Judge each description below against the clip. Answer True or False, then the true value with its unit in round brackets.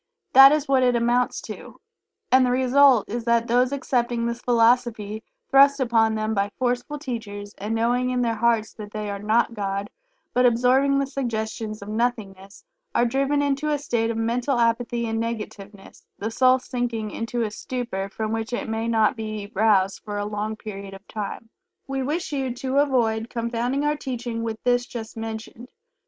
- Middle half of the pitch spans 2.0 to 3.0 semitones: True (2.6 semitones)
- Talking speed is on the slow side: False (180 wpm)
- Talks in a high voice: True (235 Hz)